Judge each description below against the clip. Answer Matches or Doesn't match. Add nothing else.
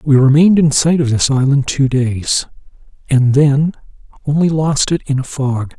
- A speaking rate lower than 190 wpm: Matches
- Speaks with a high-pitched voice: Doesn't match